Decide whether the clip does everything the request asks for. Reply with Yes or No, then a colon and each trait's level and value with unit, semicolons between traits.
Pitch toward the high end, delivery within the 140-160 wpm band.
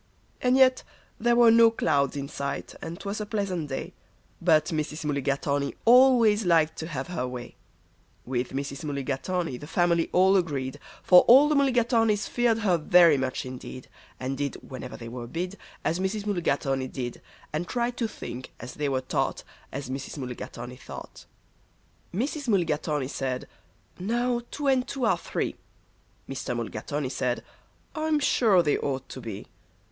No: medium, 165 Hz; average, 155 wpm